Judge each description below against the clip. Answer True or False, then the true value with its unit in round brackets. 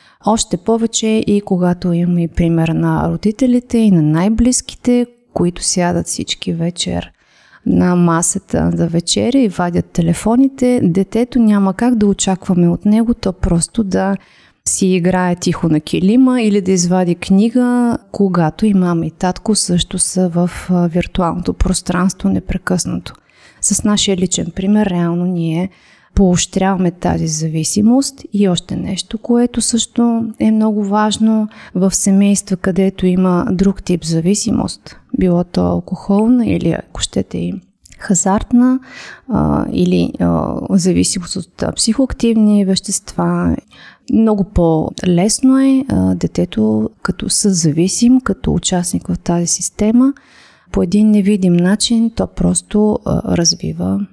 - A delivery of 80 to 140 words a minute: True (120 wpm)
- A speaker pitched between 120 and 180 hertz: False (190 Hz)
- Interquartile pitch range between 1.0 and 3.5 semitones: False (3.9 semitones)